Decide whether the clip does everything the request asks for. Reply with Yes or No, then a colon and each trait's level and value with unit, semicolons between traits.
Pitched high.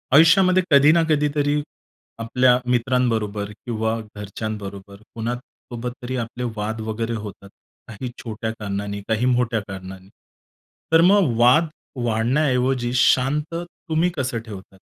No: low, 120 Hz